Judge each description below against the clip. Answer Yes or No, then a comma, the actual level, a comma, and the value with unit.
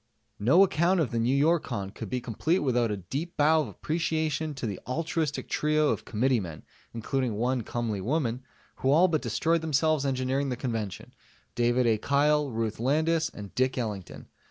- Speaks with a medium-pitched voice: No, low, 130 Hz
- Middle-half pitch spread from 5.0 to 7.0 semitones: Yes, average, 5.3 semitones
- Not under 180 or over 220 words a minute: No, average, 165 wpm